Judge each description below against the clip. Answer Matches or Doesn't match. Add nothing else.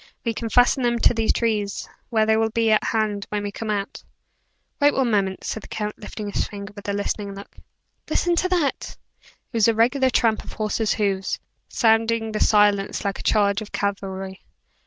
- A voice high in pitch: Matches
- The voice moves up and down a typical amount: Doesn't match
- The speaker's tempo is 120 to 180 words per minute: Doesn't match